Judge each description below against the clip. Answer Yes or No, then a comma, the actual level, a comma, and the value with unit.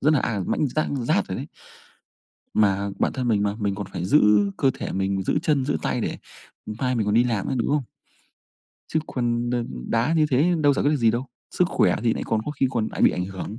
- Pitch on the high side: No, low, 120 Hz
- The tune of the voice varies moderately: Yes, average, 5.0 semitones